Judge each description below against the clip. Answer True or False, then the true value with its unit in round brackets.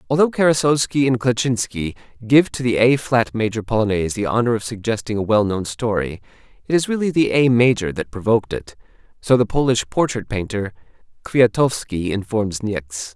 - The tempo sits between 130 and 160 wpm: True (155 wpm)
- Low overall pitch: True (115 Hz)